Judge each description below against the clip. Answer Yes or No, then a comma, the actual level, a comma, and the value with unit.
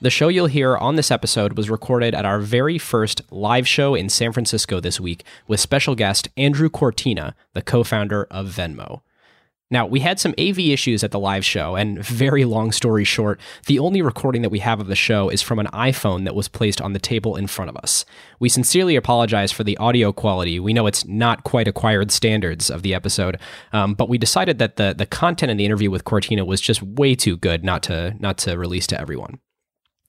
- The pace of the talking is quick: Yes, fast, 220 wpm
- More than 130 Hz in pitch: No, low, 110 Hz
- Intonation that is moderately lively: Yes, average, 4.1 semitones